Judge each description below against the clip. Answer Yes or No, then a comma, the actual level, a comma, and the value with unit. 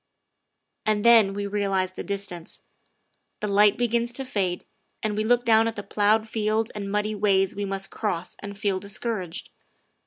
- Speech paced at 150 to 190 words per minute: Yes, average, 165 wpm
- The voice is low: No, high, 205 Hz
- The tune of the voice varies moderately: No, narrow, 1.9 semitones